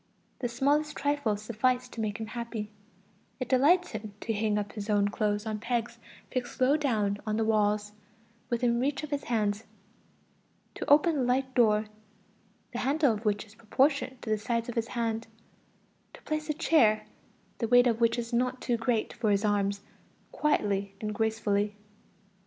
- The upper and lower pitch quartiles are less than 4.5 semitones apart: Yes, average, 3.3 semitones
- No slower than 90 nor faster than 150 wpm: No, average, 170 wpm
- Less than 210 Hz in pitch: No, high, 230 Hz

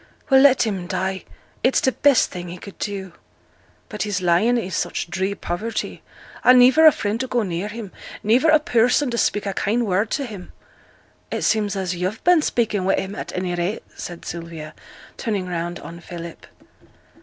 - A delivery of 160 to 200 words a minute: Yes, average, 185 wpm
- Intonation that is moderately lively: Yes, average, 4.8 semitones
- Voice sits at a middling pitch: No, high, 205 Hz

